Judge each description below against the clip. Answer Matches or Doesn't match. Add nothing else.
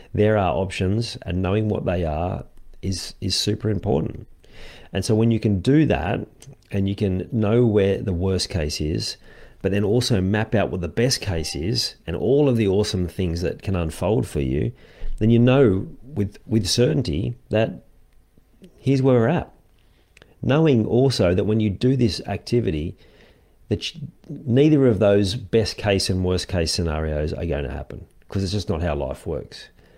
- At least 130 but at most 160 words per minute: Doesn't match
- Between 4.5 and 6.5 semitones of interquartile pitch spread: Matches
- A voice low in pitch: Matches